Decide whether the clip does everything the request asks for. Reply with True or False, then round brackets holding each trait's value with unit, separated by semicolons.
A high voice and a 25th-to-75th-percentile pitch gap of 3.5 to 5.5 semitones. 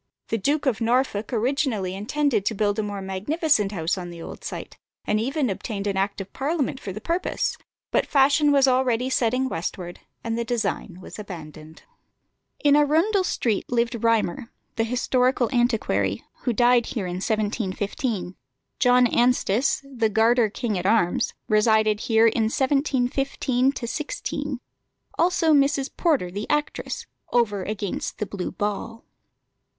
True (230 Hz; 4.6 semitones)